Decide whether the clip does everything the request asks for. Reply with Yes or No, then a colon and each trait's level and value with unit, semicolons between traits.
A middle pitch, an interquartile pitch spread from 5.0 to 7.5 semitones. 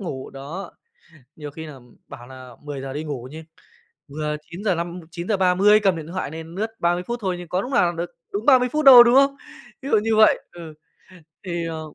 Yes: medium, 175 Hz; wide, 5.4 semitones